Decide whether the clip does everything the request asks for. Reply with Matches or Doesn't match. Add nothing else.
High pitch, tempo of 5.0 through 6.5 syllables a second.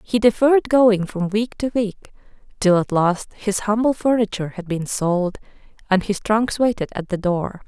Doesn't match